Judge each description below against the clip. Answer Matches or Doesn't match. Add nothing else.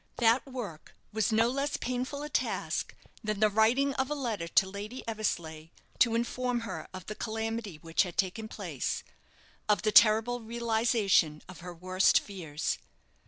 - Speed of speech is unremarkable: Matches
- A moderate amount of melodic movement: Matches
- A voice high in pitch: Matches